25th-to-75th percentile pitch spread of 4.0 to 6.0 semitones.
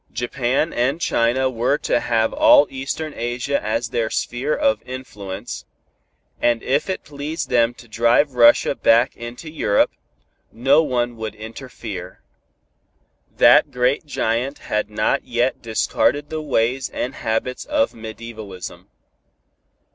No: average, 3.5 semitones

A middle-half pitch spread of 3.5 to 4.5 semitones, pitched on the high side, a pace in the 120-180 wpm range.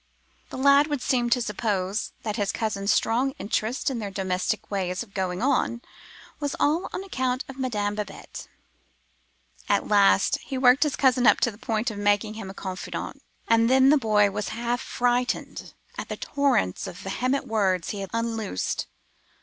Yes: average, 4.2 semitones; high, 225 Hz; average, 175 wpm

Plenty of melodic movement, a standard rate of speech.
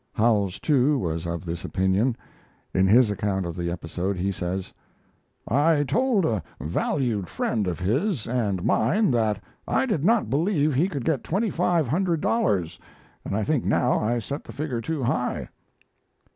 Yes: wide, 8.0 semitones; average, 165 wpm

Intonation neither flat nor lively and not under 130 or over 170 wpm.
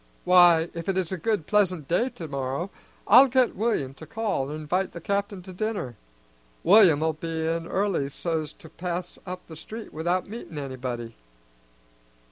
Yes: average, 4.3 semitones; average, 160 wpm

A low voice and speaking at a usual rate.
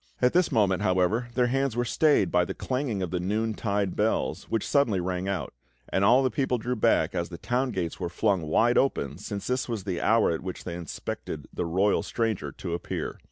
No: low, 105 Hz; fast, 215 wpm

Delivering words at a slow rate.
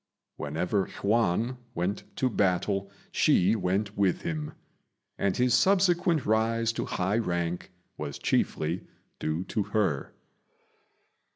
Yes: slow, 110 wpm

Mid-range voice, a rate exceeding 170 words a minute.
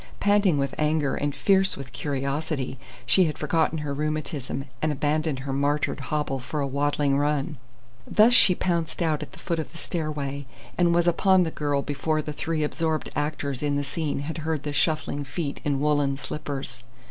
Yes: medium, 150 Hz; average, 180 wpm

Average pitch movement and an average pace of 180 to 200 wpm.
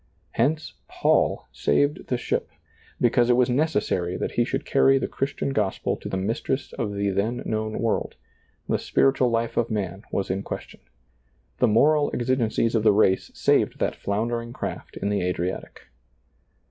No: average, 4.1 semitones; average, 170 wpm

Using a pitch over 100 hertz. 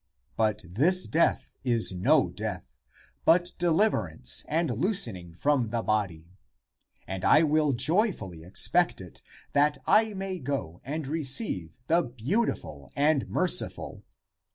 Yes: medium, 140 Hz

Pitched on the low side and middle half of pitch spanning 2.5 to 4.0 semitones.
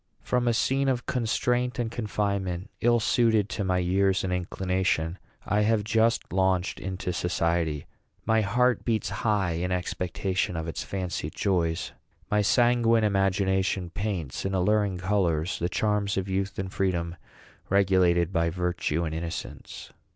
Yes: very low, 95 Hz; average, 3.1 semitones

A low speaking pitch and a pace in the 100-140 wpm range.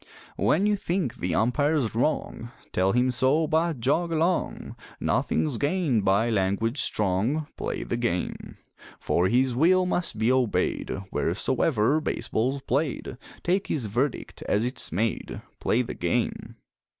Yes: low, 130 Hz; slow, 135 wpm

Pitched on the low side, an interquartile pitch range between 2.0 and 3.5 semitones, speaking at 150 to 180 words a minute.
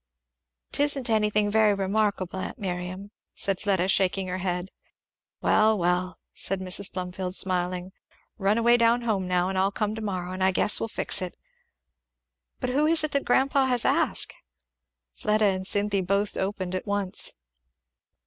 No: high, 195 Hz; average, 2.7 semitones; average, 160 wpm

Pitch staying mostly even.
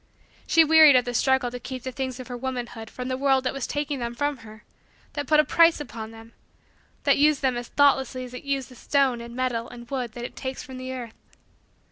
Yes: narrow, 2.3 semitones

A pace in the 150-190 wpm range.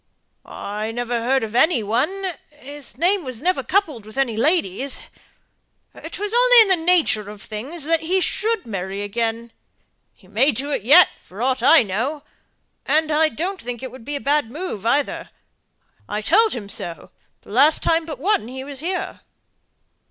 Yes: average, 175 wpm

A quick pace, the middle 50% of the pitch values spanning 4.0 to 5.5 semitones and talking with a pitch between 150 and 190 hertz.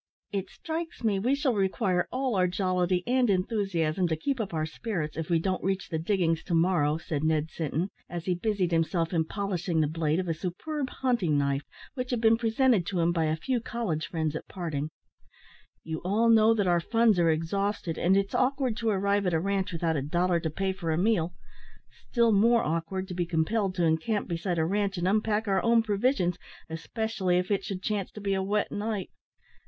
Yes: fast, 210 wpm; average, 4.6 semitones; medium, 185 Hz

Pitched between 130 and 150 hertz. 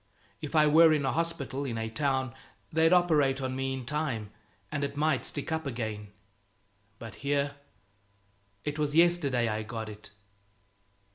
Yes: medium, 140 Hz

